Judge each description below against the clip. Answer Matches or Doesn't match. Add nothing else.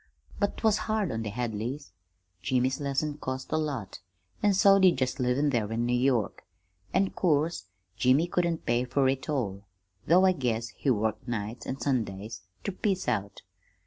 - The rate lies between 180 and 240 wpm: Doesn't match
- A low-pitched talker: Matches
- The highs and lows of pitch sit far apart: Matches